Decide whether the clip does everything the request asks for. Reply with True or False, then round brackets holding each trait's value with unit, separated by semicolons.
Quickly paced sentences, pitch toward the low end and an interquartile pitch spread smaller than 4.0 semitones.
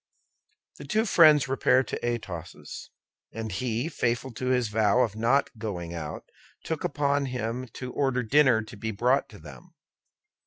False (155 wpm; 125 Hz; 3.6 semitones)